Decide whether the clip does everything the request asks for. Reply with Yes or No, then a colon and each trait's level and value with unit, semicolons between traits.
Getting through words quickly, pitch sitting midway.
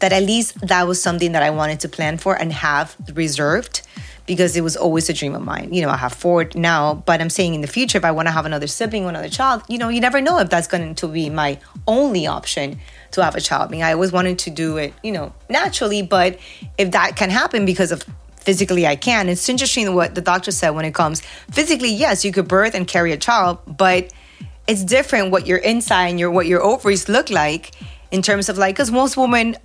Yes: fast, 245 wpm; medium, 180 Hz